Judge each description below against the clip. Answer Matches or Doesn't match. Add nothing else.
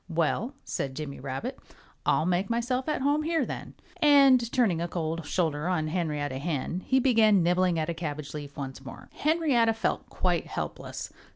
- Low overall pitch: Doesn't match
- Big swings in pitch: Matches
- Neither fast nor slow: Matches